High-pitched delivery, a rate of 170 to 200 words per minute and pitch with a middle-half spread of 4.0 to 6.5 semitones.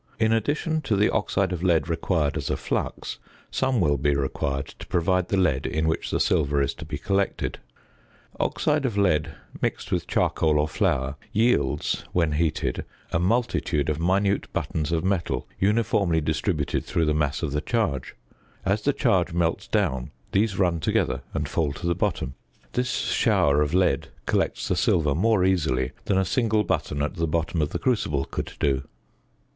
No: very low, 85 Hz; average, 175 wpm; average, 5.0 semitones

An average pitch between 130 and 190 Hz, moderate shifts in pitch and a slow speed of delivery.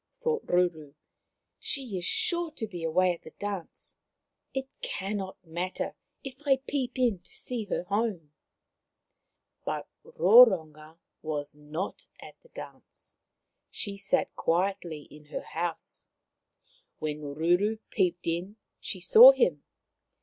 No: medium, 185 Hz; wide, 5.7 semitones; slow, 130 wpm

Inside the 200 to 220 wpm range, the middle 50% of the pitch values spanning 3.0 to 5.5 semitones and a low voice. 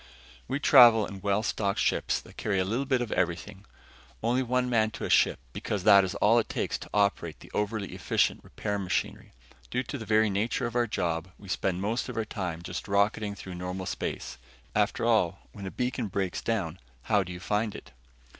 Yes: fast, 205 wpm; average, 3.3 semitones; low, 105 Hz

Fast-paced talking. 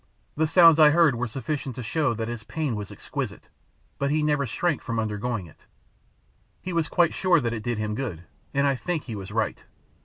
Yes: fast, 210 wpm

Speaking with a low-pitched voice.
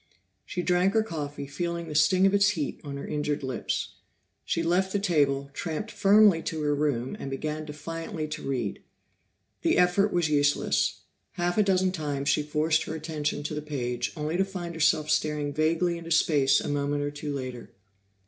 No: medium, 155 Hz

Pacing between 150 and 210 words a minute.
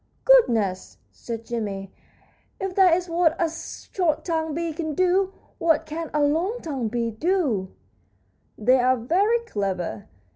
No: average, 140 wpm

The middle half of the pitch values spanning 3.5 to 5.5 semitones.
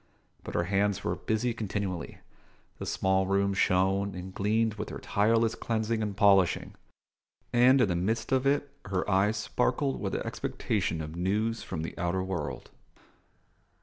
No: average, 3.1 semitones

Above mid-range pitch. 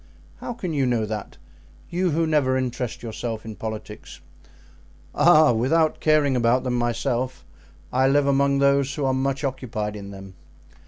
No: low, 130 Hz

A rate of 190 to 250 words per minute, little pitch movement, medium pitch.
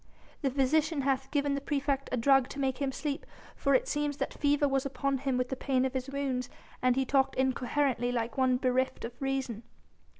No: fast, 205 wpm; narrow, 1.6 semitones; very high, 270 Hz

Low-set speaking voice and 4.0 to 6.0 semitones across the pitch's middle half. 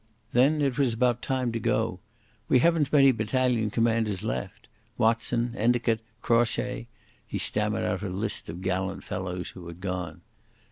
Yes: low, 115 Hz; average, 4.4 semitones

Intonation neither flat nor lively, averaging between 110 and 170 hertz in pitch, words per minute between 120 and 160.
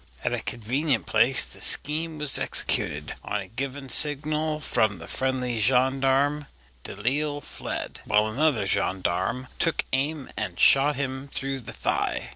Yes: average, 4.2 semitones; low, 135 Hz; average, 140 wpm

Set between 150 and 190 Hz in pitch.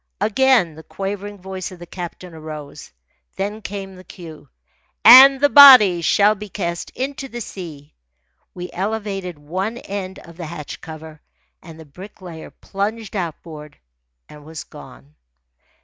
Yes: medium, 185 Hz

